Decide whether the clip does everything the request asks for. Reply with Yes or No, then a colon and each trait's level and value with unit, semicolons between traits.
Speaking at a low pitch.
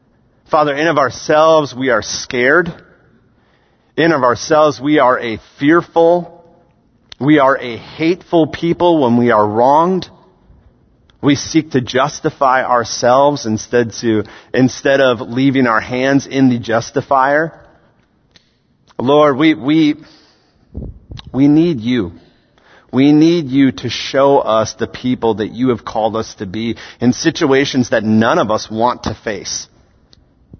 Yes: low, 130 Hz